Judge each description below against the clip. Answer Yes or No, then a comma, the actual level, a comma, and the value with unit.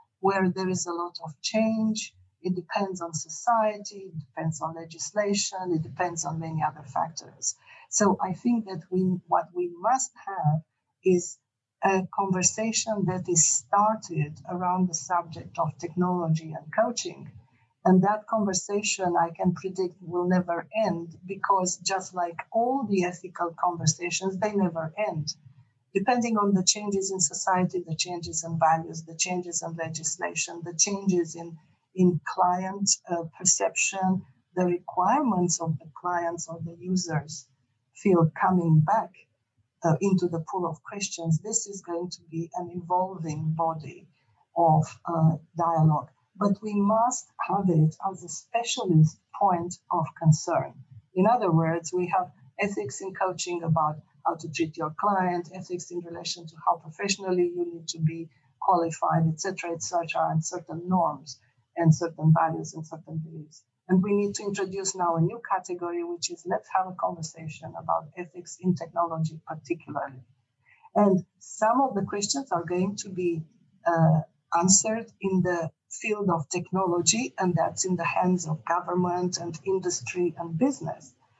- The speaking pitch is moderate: Yes, medium, 175 Hz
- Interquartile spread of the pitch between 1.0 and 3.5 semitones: Yes, average, 2.8 semitones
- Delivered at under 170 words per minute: Yes, average, 155 wpm